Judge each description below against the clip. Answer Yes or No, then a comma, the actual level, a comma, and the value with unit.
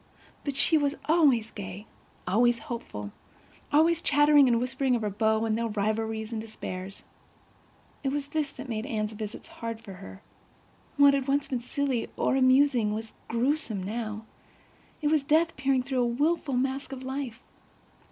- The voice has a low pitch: No, high, 245 Hz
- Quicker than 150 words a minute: Yes, average, 160 wpm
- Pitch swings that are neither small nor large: Yes, average, 4.3 semitones